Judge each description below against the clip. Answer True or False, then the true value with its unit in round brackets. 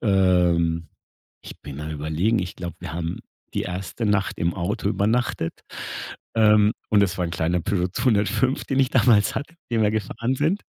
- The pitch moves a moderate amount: True (4.4 semitones)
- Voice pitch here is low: True (100 Hz)